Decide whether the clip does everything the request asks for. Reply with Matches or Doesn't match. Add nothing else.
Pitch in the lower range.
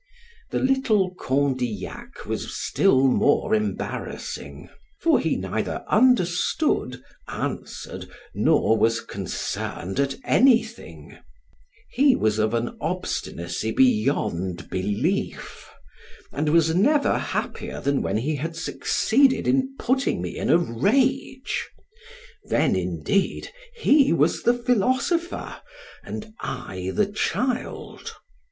Doesn't match